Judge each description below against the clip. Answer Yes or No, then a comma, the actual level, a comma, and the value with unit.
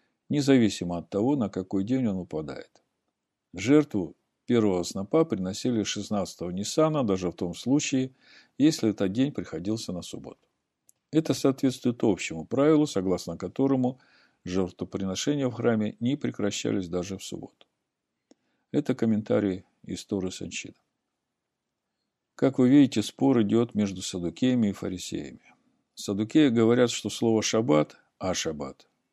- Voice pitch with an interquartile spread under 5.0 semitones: No, wide, 5.6 semitones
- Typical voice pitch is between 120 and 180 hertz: No, low, 110 Hz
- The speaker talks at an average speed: Yes, average, 120 wpm